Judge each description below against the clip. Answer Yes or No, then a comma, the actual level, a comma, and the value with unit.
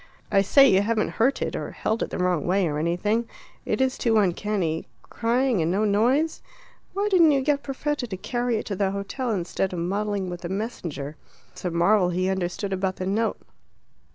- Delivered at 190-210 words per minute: Yes, average, 200 wpm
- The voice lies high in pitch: Yes, high, 200 Hz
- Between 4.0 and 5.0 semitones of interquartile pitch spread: Yes, average, 4.6 semitones